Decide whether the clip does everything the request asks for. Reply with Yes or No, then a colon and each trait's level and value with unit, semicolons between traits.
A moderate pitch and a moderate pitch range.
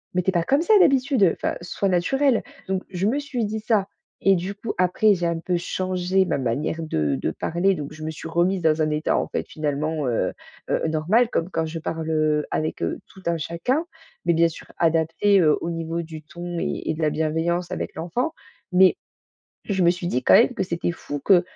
Yes: medium, 170 Hz; average, 3.4 semitones